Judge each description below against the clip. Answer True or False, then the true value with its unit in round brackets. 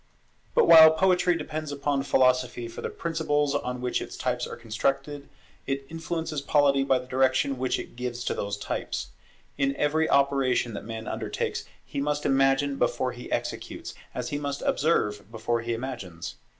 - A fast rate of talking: False (165 wpm)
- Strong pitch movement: False (3.0 semitones)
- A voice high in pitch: False (135 Hz)